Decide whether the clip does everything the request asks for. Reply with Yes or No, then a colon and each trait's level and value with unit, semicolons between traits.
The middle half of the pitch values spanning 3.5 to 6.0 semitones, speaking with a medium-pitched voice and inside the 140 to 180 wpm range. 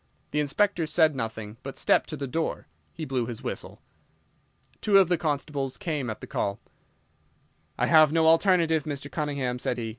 Yes: average, 4.0 semitones; medium, 150 Hz; average, 175 wpm